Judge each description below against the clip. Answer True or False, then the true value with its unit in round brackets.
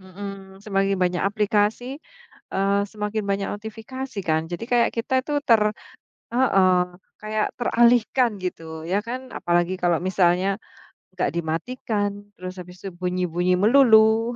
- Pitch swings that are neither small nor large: True (3.7 semitones)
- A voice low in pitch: False (200 Hz)